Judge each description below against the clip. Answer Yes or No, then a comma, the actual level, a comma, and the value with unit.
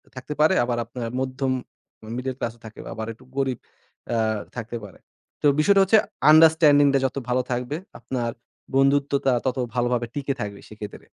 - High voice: No, low, 130 Hz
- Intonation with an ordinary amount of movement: Yes, average, 3.0 semitones